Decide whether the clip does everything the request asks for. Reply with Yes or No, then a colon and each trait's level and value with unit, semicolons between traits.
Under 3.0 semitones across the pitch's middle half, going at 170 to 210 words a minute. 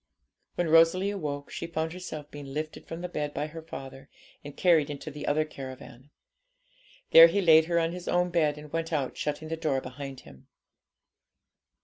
Yes: narrow, 2.5 semitones; average, 180 wpm